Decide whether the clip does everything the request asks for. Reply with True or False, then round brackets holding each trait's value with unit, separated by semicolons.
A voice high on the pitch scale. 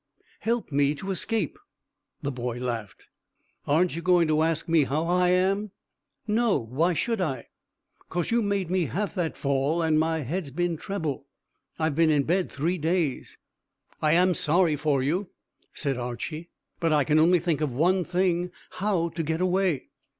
False (165 Hz)